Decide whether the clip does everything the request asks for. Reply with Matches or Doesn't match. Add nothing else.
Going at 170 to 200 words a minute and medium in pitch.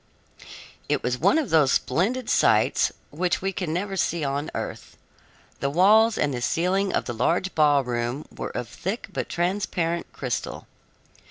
Doesn't match